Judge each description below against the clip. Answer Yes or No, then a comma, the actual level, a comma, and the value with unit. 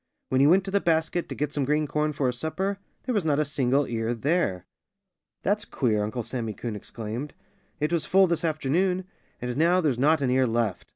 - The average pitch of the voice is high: No, medium, 145 Hz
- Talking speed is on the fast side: Yes, fast, 215 wpm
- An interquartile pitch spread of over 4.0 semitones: Yes, wide, 5.5 semitones